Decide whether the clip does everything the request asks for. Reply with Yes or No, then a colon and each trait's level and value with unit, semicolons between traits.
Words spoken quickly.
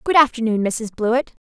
No: average, 165 wpm